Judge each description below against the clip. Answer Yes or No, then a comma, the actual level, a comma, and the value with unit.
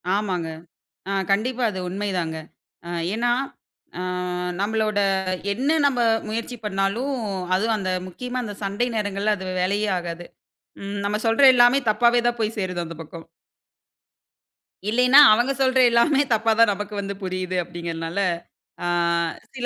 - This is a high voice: Yes, high, 210 Hz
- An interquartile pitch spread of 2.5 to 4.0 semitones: No, average, 4.4 semitones